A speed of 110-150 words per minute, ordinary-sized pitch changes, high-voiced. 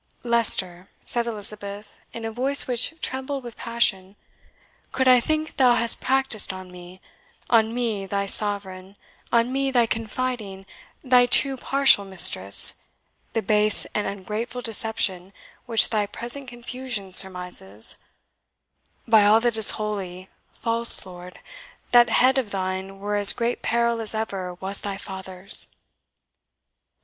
Yes: slow, 135 wpm; average, 3.9 semitones; high, 220 Hz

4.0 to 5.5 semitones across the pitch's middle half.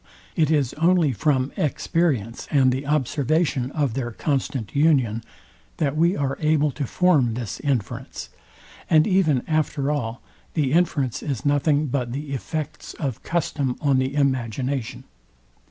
No: average, 3.2 semitones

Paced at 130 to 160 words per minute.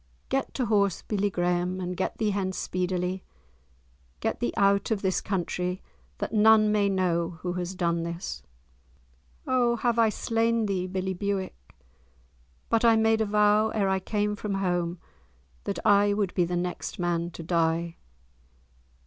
Yes: average, 155 wpm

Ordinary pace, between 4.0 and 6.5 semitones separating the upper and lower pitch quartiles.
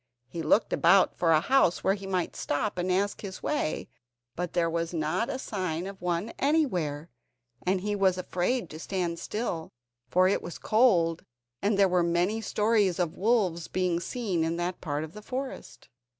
No: average, 180 wpm; average, 3.5 semitones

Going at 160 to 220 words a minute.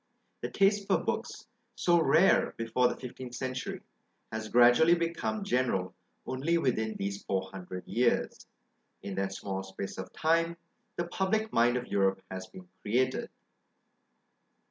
No: average, 140 wpm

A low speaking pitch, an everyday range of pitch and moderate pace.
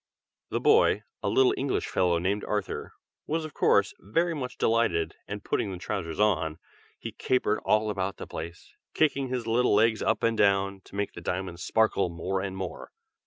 Yes: low, 100 Hz; average, 3.7 semitones; average, 180 wpm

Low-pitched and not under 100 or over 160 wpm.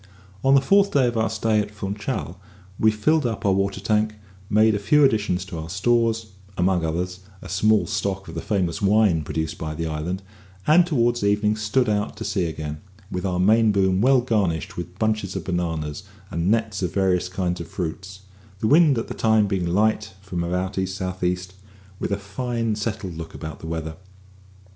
No: low, 100 Hz; average, 195 wpm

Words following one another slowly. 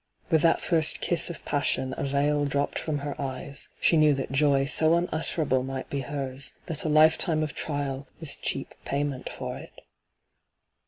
No: average, 175 wpm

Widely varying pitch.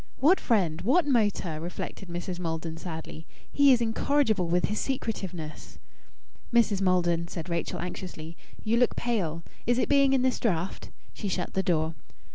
Yes: wide, 5.9 semitones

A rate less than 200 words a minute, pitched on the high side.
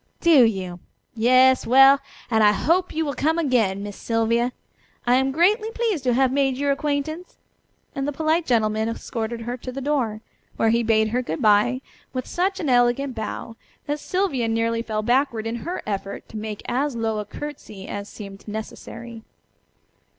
Yes: average, 175 wpm; high, 245 Hz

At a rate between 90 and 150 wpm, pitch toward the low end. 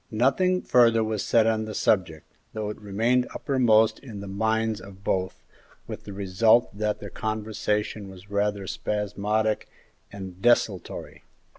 Yes: average, 140 wpm; low, 105 Hz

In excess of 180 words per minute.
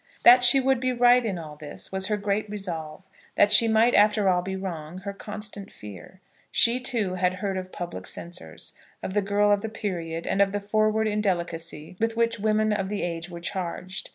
Yes: fast, 205 wpm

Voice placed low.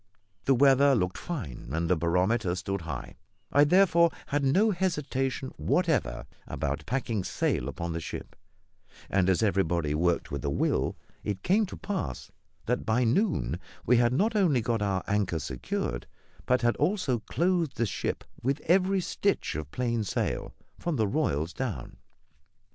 Yes: low, 120 Hz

